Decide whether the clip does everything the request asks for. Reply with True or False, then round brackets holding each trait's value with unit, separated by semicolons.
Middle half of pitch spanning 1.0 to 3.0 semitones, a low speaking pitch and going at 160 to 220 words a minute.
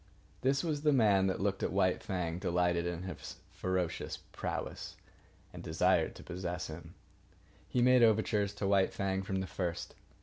True (2.7 semitones; 95 Hz; 165 wpm)